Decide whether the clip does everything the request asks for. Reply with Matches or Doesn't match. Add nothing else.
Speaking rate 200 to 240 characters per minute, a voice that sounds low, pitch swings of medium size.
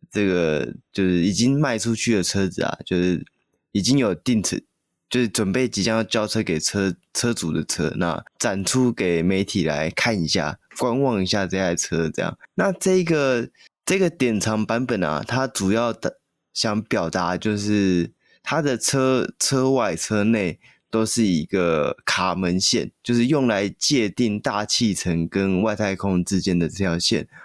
Matches